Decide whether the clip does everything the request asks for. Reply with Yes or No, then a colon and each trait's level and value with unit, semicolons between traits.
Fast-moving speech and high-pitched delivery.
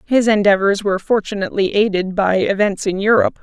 No: average, 160 wpm; high, 200 Hz